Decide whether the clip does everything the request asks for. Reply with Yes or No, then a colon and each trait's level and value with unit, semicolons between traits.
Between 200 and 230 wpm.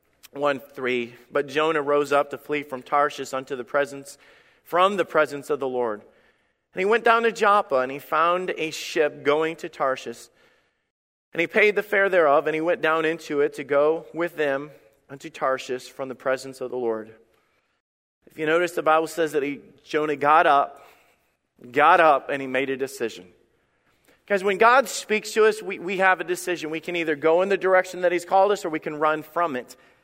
Yes: fast, 205 wpm